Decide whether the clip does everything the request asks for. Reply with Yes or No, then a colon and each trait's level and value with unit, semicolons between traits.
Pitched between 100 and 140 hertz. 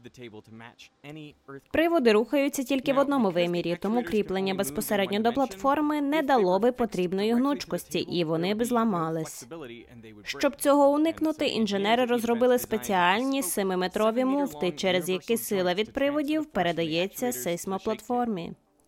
No: high, 215 Hz